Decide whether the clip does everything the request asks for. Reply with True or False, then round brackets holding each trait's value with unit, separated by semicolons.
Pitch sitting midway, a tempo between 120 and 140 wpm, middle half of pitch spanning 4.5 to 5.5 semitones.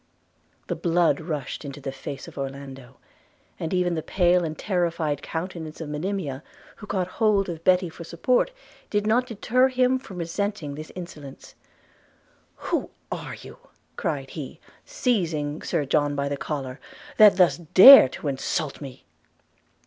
False (165 Hz; 150 wpm; 5.0 semitones)